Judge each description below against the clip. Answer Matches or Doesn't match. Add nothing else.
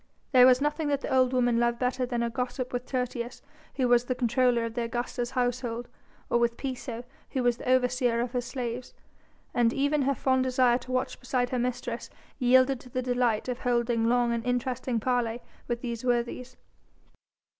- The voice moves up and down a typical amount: Doesn't match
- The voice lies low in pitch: Doesn't match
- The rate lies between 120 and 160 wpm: Doesn't match